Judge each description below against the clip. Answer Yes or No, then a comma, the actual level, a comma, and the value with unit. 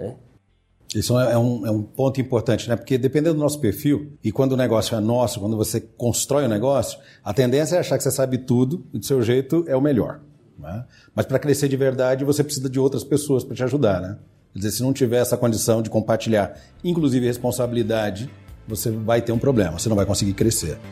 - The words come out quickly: Yes, fast, 220 wpm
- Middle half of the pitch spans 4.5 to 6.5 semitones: No, average, 3.6 semitones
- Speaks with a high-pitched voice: No, low, 120 Hz